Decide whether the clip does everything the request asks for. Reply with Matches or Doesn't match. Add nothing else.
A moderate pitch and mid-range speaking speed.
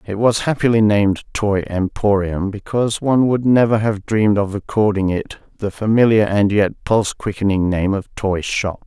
Doesn't match